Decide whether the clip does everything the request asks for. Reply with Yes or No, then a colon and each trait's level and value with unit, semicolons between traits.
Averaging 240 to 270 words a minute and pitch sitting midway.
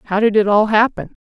No: fast, 245 wpm; high, 210 Hz